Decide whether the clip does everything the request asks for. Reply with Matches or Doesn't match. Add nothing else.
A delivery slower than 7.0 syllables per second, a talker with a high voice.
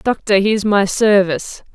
Matches